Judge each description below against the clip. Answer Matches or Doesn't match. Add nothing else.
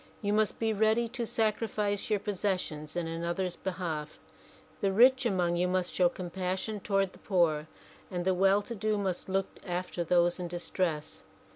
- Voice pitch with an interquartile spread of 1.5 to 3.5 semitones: Matches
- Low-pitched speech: Doesn't match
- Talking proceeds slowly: Doesn't match